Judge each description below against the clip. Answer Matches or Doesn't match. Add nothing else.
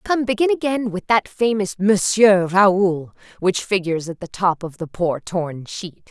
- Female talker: Matches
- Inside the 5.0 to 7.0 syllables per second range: Doesn't match